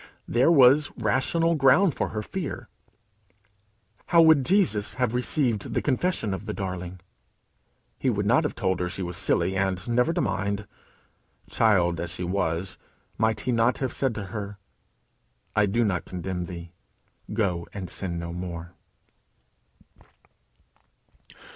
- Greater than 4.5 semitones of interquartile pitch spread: Yes, wide, 5.6 semitones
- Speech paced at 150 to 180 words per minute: No, average, 140 wpm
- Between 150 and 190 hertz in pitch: No, low, 105 Hz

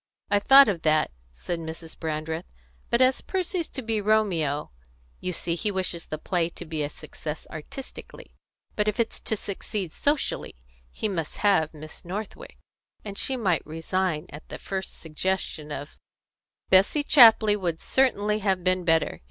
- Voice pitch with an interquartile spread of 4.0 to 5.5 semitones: Yes, average, 4.9 semitones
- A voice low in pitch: No, medium, 185 Hz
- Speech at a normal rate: Yes, average, 160 wpm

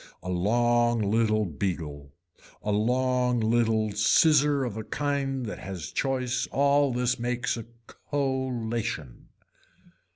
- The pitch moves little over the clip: No, average, 3.5 semitones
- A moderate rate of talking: No, slow, 110 wpm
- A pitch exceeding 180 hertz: No, low, 120 Hz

